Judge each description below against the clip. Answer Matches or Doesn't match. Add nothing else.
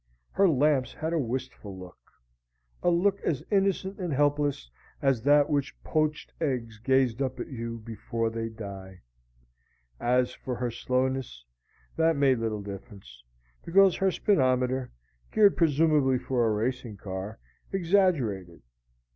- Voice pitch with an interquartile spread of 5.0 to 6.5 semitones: Matches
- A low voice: Matches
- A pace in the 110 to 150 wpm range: Matches